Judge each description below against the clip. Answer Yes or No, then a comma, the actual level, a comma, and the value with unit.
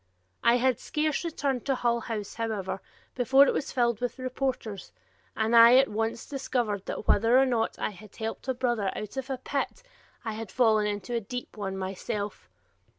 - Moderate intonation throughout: Yes, average, 3.3 semitones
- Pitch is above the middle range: Yes, high, 235 Hz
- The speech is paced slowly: No, average, 185 wpm